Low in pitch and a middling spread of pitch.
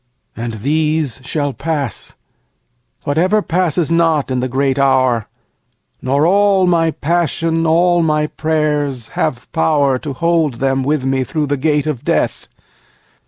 No: medium, 150 Hz; average, 3.6 semitones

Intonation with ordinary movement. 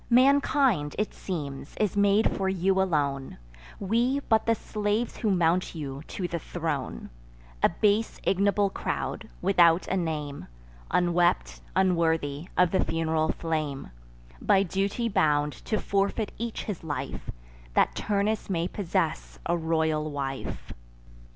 Yes: average, 4.3 semitones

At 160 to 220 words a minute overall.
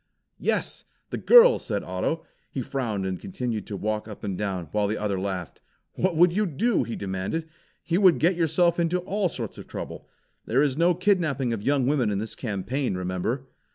Yes: average, 190 wpm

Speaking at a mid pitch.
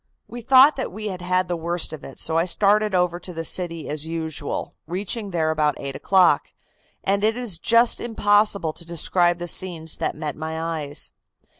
Yes: medium, 175 Hz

